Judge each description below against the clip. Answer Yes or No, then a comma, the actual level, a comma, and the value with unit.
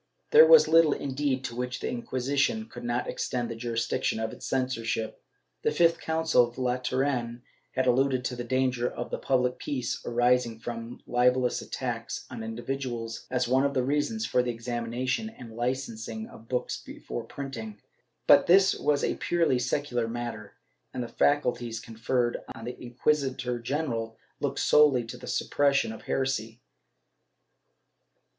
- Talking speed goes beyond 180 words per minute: No, average, 155 wpm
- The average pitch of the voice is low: Yes, low, 125 Hz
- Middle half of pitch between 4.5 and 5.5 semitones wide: No, narrow, 2.4 semitones